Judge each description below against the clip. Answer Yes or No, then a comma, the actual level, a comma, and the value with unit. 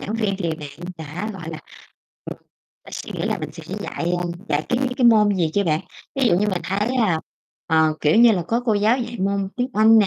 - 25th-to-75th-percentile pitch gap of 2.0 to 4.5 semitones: No, average, 5.1 semitones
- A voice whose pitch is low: No, high, 200 Hz